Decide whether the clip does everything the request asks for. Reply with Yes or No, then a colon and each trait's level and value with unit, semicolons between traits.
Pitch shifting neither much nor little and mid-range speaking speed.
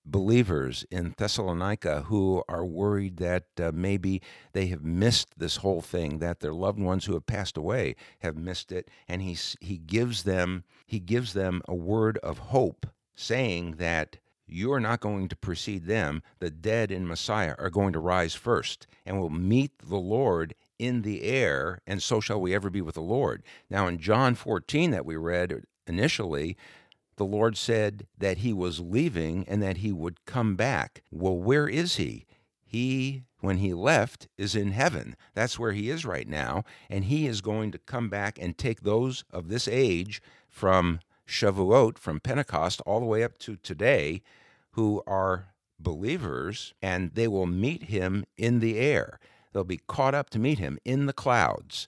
Yes: average, 4.1 semitones; average, 180 wpm